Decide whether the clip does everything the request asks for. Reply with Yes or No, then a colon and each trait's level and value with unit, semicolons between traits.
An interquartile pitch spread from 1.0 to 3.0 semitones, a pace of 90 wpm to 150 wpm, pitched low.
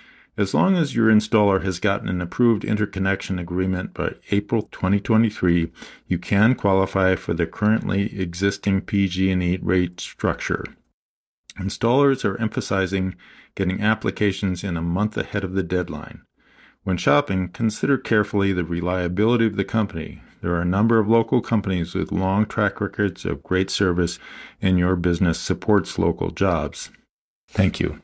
Yes: average, 2.7 semitones; average, 145 wpm; very low, 95 Hz